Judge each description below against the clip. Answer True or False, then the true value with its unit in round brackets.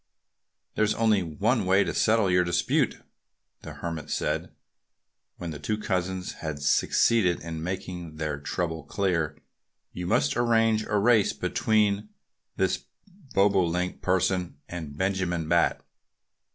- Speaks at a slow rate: True (125 wpm)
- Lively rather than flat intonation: False (3.8 semitones)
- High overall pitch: False (90 Hz)